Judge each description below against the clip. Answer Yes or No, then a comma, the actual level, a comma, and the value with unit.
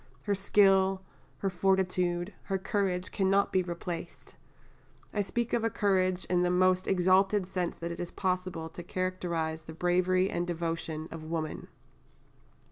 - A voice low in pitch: No, medium, 185 Hz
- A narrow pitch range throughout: Yes, narrow, 1.8 semitones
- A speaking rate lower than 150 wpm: Yes, average, 140 wpm